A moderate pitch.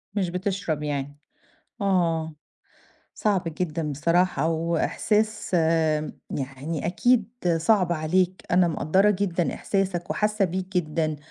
Yes: medium, 175 Hz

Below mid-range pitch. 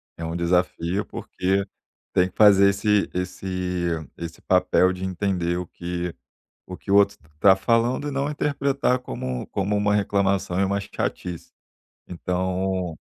Yes: very low, 95 Hz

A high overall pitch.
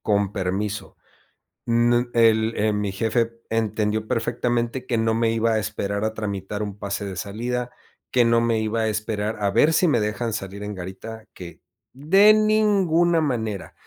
No: low, 110 Hz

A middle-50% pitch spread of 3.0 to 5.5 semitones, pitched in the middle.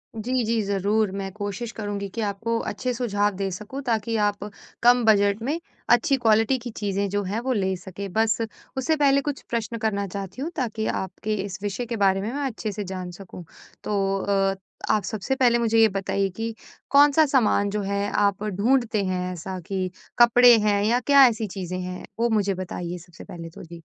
No: average, 3.3 semitones; high, 210 Hz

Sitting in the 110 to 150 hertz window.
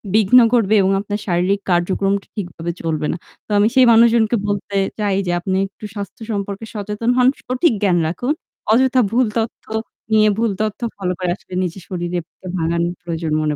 No: high, 200 Hz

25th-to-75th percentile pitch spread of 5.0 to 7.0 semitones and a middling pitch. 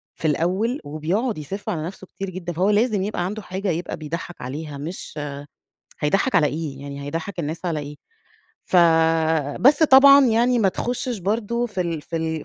Yes: wide, 5.6 semitones; medium, 180 Hz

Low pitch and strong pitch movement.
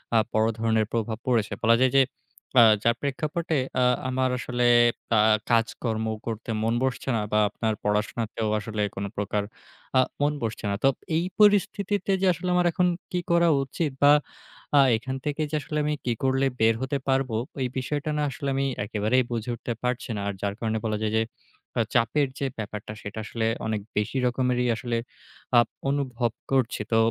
No: low, 120 Hz; average, 3.8 semitones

